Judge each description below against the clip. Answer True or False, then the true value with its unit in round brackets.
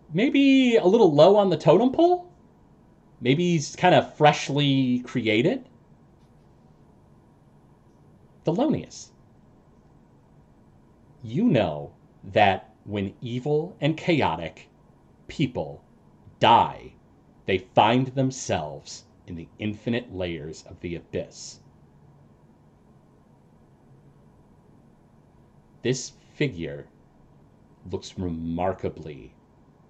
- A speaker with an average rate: False (75 wpm)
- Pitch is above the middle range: False (125 Hz)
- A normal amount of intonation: False (8.5 semitones)